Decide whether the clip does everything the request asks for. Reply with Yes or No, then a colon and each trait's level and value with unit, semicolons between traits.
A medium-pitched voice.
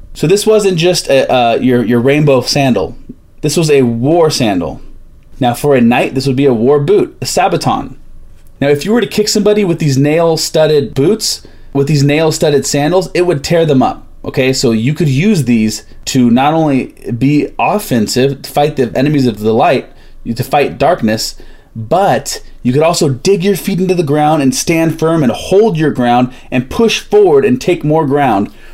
Yes: medium, 145 Hz